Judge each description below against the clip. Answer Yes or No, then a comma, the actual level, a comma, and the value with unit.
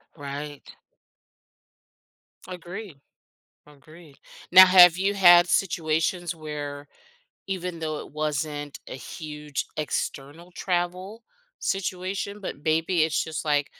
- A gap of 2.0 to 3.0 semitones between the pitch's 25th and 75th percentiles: No, average, 3.4 semitones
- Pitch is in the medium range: Yes, medium, 165 Hz